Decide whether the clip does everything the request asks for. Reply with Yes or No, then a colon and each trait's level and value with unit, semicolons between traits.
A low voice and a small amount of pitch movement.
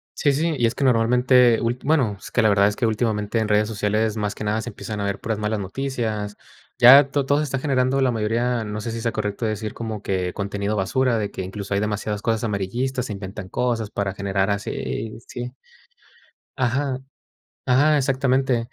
No: low, 110 Hz; average, 3.4 semitones